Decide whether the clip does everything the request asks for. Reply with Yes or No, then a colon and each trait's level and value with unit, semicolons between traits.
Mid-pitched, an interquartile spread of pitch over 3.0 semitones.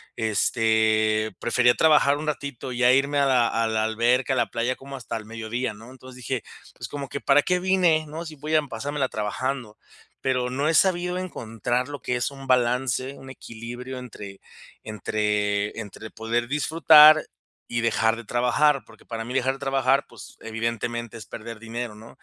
No: low, 125 Hz; average, 3.6 semitones